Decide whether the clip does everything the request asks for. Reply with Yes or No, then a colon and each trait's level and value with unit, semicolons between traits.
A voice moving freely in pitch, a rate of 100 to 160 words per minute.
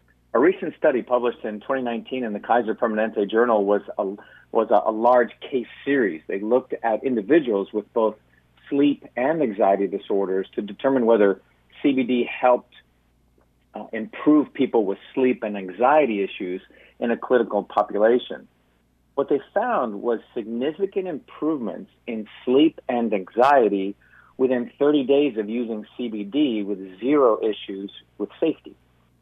No: average, 4.3 semitones; average, 140 wpm